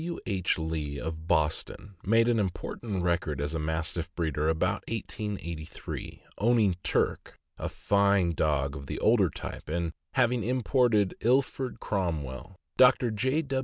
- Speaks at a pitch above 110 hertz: No, very low, 95 Hz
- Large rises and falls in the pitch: Yes, wide, 6.1 semitones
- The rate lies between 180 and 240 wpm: No, slow, 135 wpm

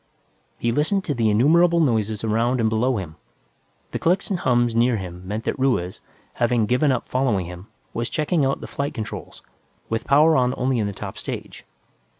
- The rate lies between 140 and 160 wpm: No, average, 185 wpm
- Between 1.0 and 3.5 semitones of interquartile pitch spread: No, average, 4.2 semitones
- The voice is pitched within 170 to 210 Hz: No, low, 120 Hz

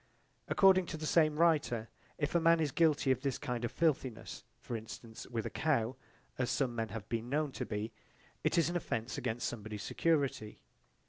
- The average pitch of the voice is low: Yes, low, 130 Hz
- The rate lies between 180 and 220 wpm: Yes, average, 190 wpm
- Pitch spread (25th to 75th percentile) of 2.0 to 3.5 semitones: No, wide, 5.6 semitones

